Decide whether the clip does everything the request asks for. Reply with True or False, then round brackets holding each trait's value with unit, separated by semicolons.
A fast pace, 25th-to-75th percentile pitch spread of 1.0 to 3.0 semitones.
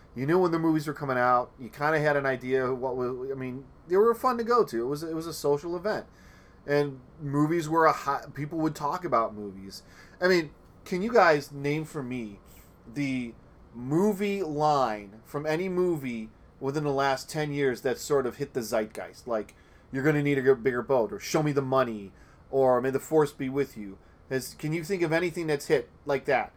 False (215 wpm; 4.1 semitones)